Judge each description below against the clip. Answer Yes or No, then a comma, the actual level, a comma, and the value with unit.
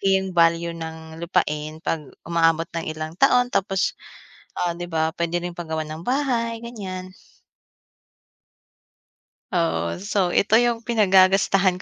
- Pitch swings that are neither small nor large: Yes, average, 3.3 semitones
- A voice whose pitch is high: No, medium, 175 Hz